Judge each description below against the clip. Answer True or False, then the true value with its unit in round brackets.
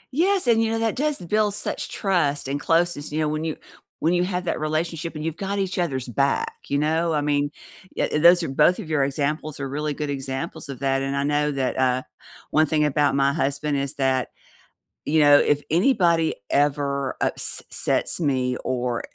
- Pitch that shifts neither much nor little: True (3.5 semitones)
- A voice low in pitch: False (150 Hz)